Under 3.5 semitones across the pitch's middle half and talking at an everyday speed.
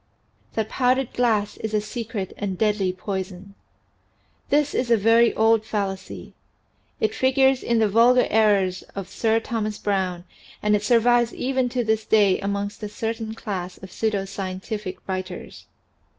Yes: average, 2.8 semitones; average, 150 wpm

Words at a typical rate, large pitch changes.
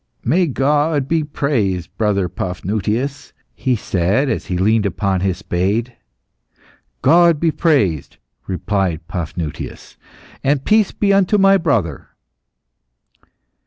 No: slow, 110 wpm; wide, 8.1 semitones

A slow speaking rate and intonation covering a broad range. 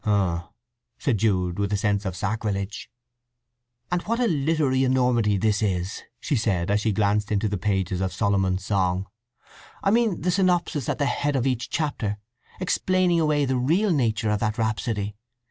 No: average, 170 wpm; wide, 6.3 semitones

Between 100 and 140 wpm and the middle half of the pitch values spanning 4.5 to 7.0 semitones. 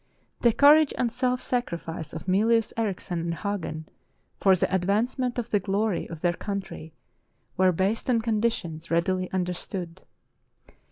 Yes: slow, 135 wpm; average, 4.8 semitones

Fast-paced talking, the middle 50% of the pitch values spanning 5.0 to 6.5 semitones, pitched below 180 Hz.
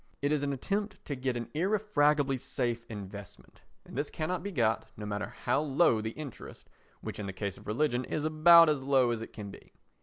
Yes: fast, 210 wpm; wide, 5.6 semitones; low, 135 Hz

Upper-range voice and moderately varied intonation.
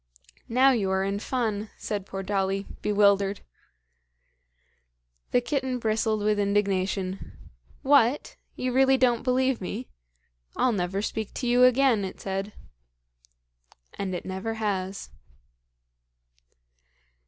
Yes: high, 210 Hz; average, 4.1 semitones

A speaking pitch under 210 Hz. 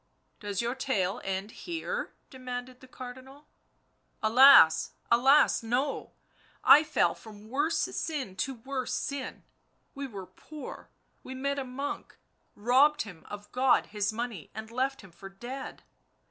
No: very high, 255 Hz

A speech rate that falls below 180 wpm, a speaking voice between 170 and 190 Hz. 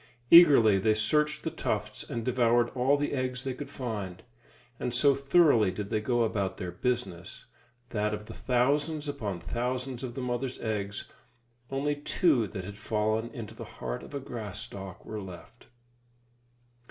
No: average, 165 wpm; low, 120 Hz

